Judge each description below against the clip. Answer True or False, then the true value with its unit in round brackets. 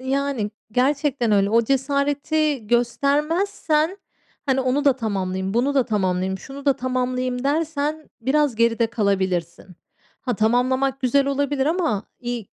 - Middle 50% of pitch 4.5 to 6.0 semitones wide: False (3.9 semitones)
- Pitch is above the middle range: True (260 Hz)